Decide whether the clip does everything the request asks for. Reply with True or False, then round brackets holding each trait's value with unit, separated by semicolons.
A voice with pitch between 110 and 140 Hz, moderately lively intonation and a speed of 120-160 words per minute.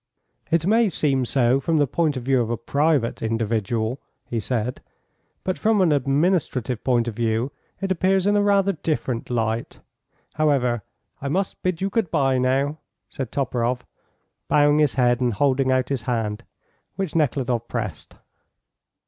True (135 Hz; 4.9 semitones; 155 wpm)